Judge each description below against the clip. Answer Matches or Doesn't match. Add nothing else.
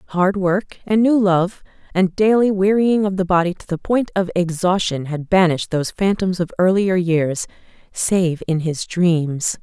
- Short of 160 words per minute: Doesn't match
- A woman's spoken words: Matches